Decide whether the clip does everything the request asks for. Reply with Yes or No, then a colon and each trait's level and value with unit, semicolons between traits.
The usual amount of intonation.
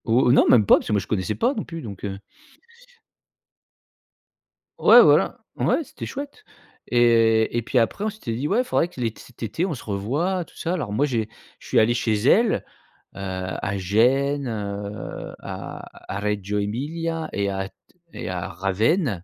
No: wide, 7.3 semitones